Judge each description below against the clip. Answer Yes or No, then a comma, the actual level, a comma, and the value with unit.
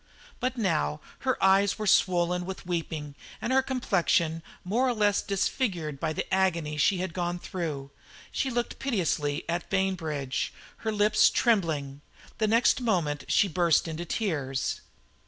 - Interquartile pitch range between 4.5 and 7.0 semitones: Yes, average, 5.0 semitones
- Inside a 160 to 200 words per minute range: No, average, 145 wpm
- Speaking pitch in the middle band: Yes, medium, 180 Hz